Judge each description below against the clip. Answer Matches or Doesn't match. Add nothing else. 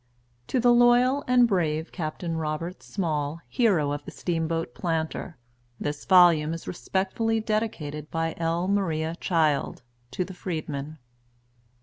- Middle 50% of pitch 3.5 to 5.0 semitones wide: Matches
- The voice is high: Doesn't match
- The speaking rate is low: Matches